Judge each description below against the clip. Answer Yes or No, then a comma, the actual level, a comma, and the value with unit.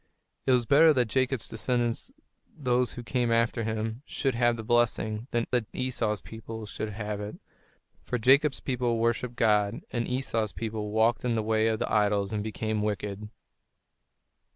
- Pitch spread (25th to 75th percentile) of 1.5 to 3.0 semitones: Yes, narrow, 2.4 semitones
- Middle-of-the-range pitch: No, low, 115 Hz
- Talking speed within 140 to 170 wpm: Yes, average, 165 wpm